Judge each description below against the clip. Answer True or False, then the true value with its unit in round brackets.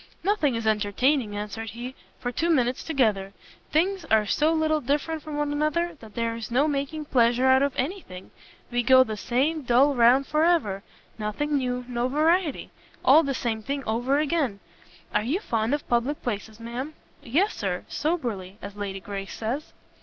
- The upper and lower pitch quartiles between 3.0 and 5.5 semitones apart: True (5.2 semitones)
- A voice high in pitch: True (255 Hz)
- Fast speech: False (175 wpm)